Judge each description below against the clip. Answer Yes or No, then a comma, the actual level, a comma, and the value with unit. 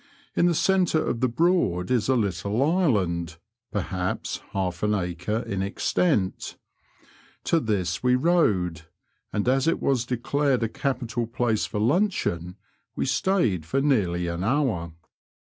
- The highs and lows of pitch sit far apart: Yes, wide, 7.1 semitones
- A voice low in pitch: Yes, low, 115 Hz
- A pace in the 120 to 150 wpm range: Yes, average, 140 wpm